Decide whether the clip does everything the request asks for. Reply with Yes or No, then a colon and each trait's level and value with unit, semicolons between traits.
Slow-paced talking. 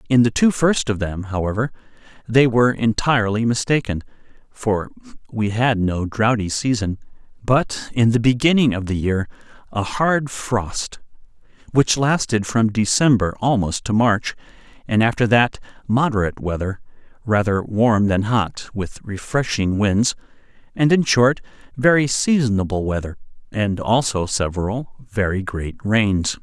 Yes: slow, 130 wpm